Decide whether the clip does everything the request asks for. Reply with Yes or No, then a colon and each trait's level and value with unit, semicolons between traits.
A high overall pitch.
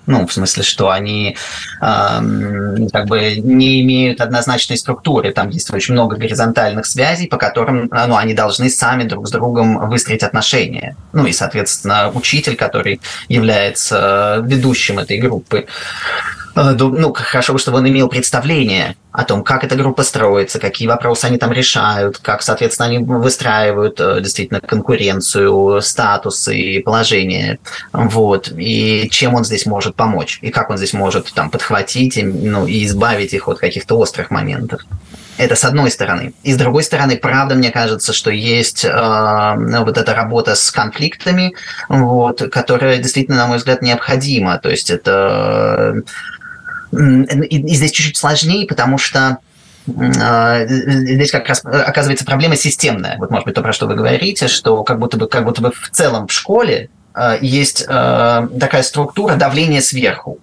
No: low, 120 Hz